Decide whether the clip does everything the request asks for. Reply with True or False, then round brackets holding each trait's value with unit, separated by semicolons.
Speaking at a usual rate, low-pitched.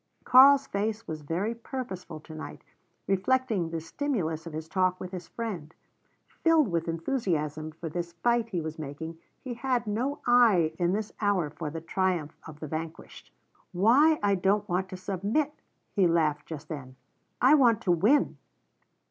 False (160 wpm; 185 Hz)